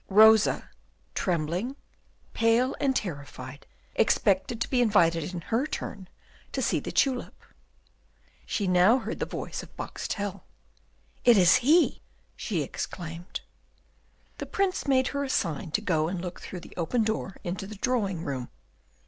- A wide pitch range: Yes, wide, 5.9 semitones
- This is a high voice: Yes, high, 195 Hz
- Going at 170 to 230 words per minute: No, average, 145 wpm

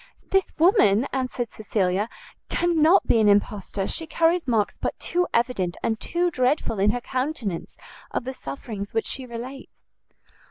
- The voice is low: No, high, 245 Hz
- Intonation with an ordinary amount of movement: No, wide, 7.0 semitones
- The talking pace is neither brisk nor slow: Yes, average, 150 wpm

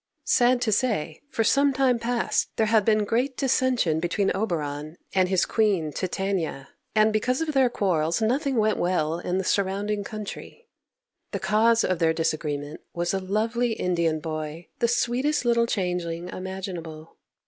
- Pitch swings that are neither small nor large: No, wide, 5.7 semitones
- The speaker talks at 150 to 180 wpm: Yes, average, 155 wpm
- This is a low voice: No, high, 200 Hz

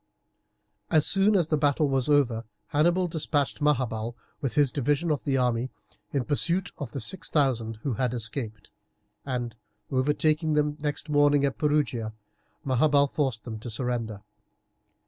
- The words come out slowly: No, average, 145 wpm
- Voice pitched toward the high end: No, medium, 140 Hz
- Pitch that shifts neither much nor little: Yes, average, 3.7 semitones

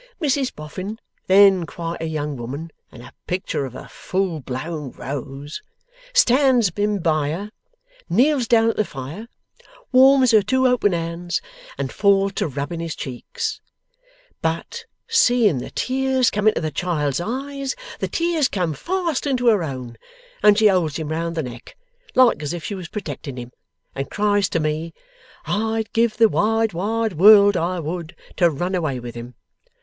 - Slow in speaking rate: No, average, 165 wpm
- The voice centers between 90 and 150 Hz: No, medium, 185 Hz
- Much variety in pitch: Yes, wide, 6.7 semitones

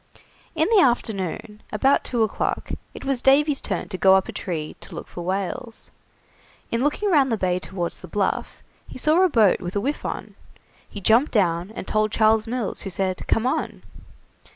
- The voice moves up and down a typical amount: No, wide, 5.7 semitones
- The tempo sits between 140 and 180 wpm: No, average, 190 wpm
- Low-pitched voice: No, high, 215 Hz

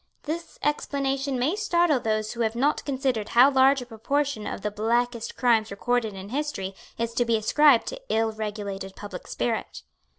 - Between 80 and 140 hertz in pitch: No, high, 240 Hz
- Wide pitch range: No, average, 4.3 semitones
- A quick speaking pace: No, average, 170 wpm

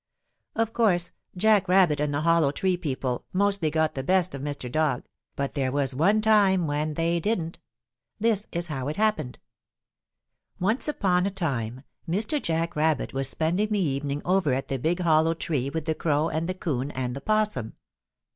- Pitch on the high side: No, medium, 160 Hz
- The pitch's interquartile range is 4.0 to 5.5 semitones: Yes, average, 5.0 semitones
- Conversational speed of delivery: Yes, average, 180 wpm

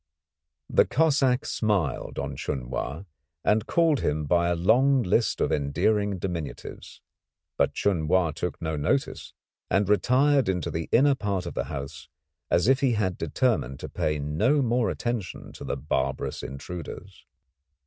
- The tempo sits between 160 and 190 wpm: No, average, 150 wpm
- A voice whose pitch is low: Yes, very low, 95 Hz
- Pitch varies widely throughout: Yes, wide, 8.0 semitones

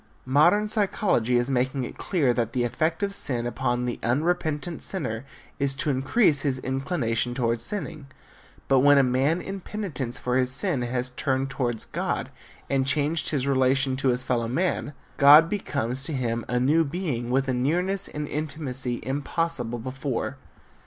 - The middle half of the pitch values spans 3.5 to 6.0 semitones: Yes, average, 4.0 semitones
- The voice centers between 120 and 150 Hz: Yes, low, 135 Hz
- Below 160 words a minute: No, average, 165 wpm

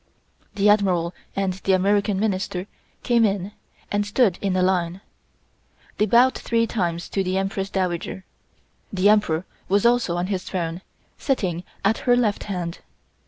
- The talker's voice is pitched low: No, high, 195 Hz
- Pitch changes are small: Yes, narrow, 2.3 semitones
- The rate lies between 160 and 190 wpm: No, average, 150 wpm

